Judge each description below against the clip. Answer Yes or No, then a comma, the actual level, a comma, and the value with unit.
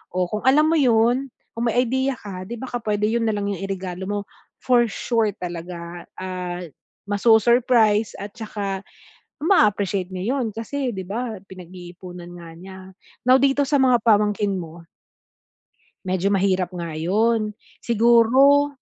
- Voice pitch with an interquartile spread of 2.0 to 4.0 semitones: No, average, 4.5 semitones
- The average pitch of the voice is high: Yes, high, 210 Hz